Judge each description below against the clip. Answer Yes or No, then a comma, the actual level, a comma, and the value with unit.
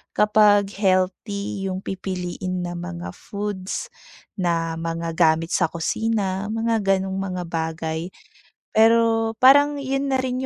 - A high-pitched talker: Yes, high, 195 Hz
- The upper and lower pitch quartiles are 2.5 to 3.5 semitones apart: No, average, 4.2 semitones